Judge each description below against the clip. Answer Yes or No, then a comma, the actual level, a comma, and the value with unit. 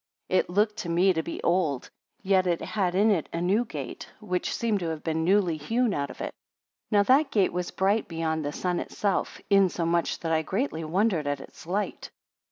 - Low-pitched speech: No, medium, 180 Hz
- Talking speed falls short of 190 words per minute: No, fast, 205 wpm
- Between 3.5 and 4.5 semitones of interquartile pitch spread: Yes, average, 3.9 semitones